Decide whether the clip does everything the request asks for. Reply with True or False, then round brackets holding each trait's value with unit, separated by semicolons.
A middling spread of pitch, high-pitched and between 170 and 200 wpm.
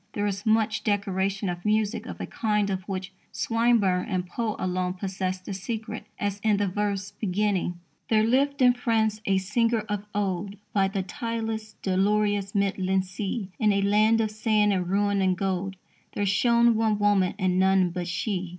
False (2.3 semitones; 205 Hz; 175 wpm)